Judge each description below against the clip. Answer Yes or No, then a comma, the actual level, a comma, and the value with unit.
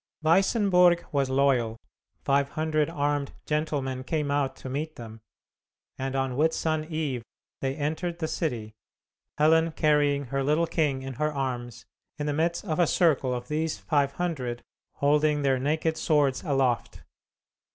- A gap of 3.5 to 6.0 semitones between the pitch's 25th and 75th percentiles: No, average, 3.1 semitones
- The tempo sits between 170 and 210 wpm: No, average, 145 wpm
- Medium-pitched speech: Yes, medium, 145 Hz